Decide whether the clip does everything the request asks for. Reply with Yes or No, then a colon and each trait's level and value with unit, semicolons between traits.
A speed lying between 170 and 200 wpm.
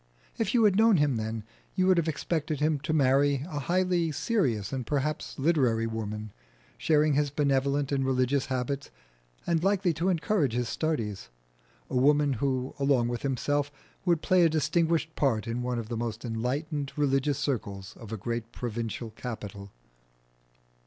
No: average, 160 wpm